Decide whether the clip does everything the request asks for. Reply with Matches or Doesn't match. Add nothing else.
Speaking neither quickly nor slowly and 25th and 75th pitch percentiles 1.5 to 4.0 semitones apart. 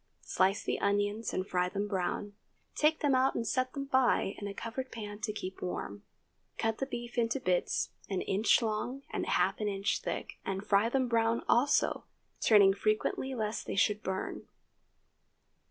Matches